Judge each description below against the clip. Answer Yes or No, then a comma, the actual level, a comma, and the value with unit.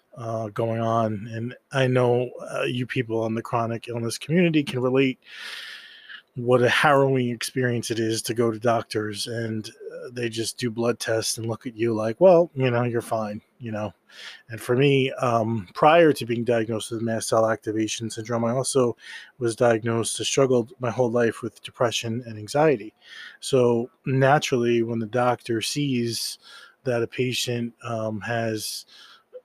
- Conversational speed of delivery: Yes, average, 165 wpm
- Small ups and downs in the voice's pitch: Yes, narrow, 2.2 semitones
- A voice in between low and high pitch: No, low, 120 Hz